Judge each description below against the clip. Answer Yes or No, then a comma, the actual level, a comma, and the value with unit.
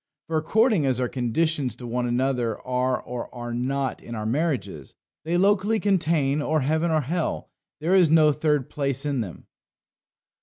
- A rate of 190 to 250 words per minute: No, average, 165 wpm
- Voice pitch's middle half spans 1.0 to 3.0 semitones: No, average, 4.6 semitones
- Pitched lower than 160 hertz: Yes, medium, 140 Hz